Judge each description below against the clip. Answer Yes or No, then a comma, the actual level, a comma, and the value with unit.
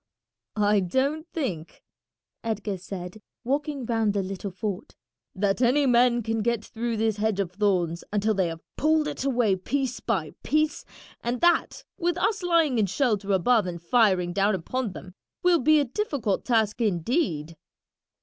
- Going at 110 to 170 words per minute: Yes, average, 160 wpm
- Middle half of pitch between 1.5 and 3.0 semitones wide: No, average, 5.3 semitones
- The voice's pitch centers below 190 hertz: No, high, 220 Hz